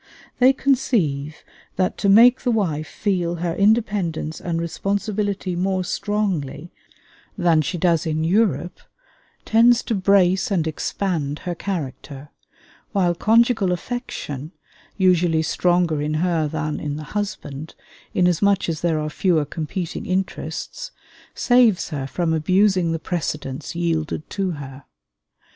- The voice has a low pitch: No, medium, 175 Hz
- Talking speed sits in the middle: No, slow, 125 wpm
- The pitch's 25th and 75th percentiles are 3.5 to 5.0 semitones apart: Yes, average, 4.3 semitones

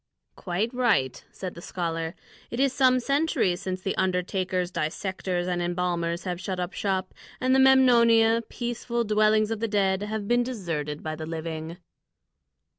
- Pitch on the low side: No, high, 190 Hz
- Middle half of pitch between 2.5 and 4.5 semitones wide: No, average, 4.9 semitones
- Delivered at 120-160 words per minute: Yes, average, 155 wpm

